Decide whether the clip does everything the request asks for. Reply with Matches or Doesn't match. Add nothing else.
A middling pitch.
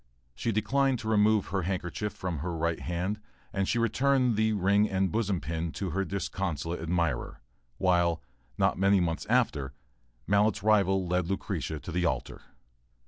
Doesn't match